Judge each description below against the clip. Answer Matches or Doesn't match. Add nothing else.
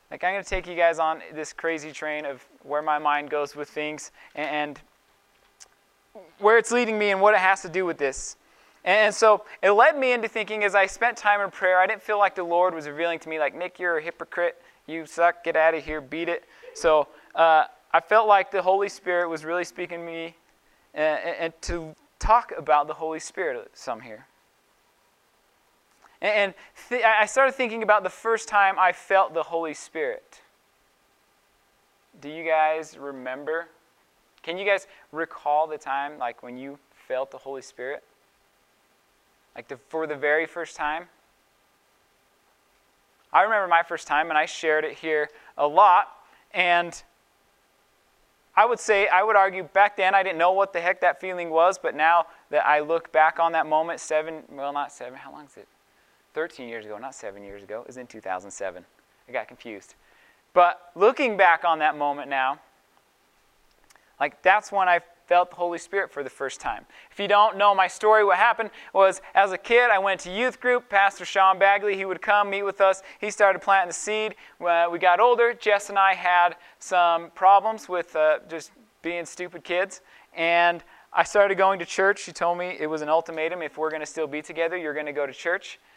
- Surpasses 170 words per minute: Matches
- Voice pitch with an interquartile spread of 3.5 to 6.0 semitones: Matches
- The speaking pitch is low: Doesn't match